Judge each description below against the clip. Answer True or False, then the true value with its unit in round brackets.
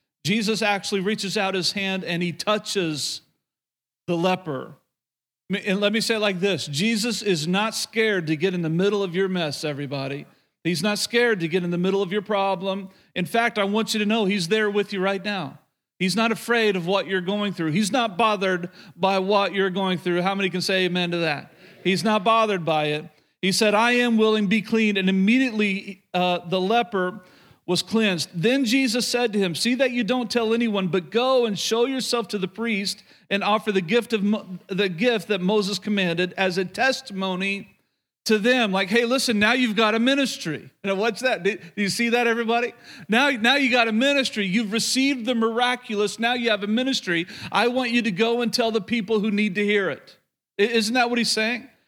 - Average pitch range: True (3.3 semitones)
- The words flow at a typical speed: False (210 wpm)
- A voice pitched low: False (205 Hz)